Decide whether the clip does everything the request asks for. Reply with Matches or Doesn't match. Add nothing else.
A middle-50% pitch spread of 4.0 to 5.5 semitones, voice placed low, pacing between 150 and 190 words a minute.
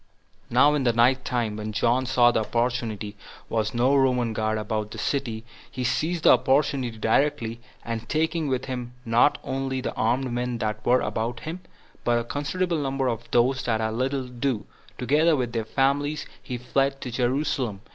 Doesn't match